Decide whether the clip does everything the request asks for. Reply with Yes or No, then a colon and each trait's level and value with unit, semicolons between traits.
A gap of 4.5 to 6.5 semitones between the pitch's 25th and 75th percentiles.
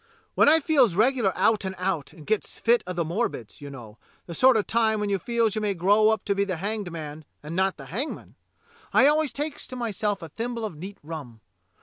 Yes: wide, 5.6 semitones